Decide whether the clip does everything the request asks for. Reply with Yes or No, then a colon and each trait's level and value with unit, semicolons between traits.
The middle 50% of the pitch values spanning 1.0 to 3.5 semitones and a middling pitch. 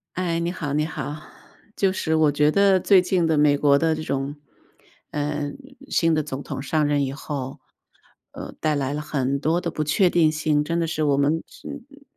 Yes: narrow, 2.5 semitones; medium, 155 Hz